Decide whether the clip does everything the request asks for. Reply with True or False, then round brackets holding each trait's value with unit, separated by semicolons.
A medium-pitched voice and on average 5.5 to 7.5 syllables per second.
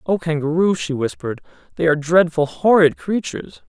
True (150 Hz; 5.6 syllables/s)